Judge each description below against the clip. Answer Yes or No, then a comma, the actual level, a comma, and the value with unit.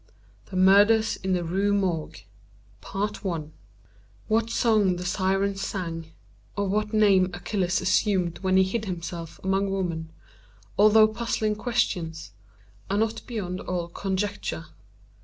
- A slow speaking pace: Yes, slow, 120 wpm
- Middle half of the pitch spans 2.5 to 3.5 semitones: Yes, average, 3.1 semitones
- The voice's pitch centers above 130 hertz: Yes, high, 190 Hz